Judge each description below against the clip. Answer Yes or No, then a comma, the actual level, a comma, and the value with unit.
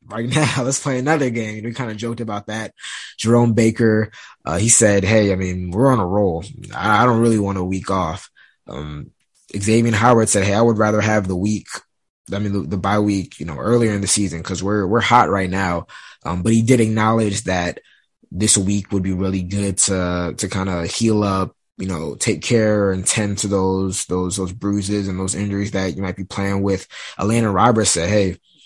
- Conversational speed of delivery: No, fast, 220 wpm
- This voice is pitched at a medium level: No, low, 100 Hz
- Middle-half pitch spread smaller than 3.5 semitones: Yes, average, 2.9 semitones